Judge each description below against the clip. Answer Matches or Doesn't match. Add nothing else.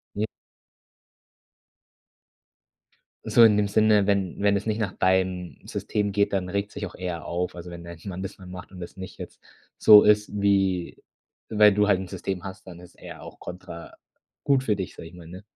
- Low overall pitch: Matches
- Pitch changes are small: Matches